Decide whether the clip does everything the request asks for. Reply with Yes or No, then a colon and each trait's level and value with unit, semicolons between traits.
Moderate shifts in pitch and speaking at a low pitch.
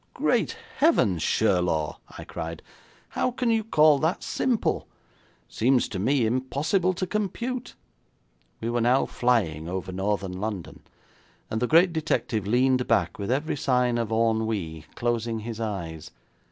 No: wide, 6.5 semitones; low, 115 Hz